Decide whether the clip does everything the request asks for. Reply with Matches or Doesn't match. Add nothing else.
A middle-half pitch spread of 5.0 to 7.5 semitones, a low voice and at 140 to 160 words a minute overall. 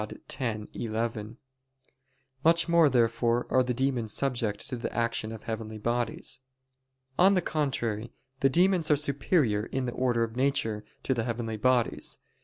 Doesn't match